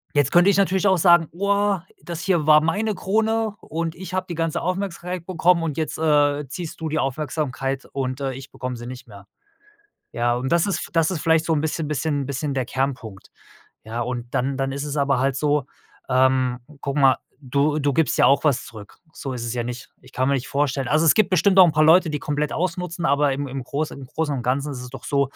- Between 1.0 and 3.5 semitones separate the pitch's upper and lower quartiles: No, average, 4.1 semitones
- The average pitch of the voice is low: No, medium, 145 Hz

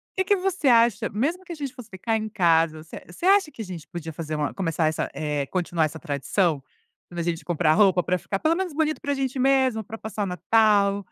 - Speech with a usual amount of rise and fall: No, wide, 8.2 semitones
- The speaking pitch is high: Yes, high, 200 Hz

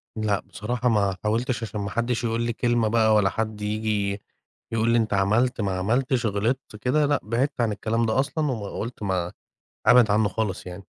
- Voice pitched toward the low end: Yes, low, 110 Hz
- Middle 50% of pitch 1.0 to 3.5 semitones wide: Yes, narrow, 2.5 semitones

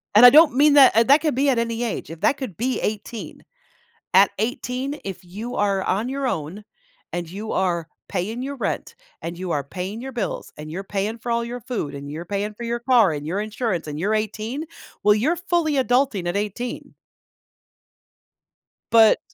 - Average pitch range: Yes, average, 4.8 semitones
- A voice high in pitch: Yes, high, 220 Hz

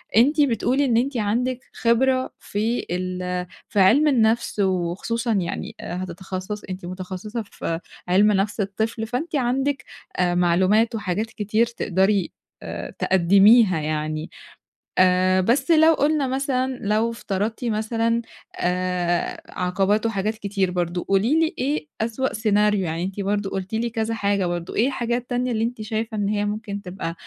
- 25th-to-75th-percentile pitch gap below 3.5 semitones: No, average, 4.1 semitones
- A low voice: No, high, 210 Hz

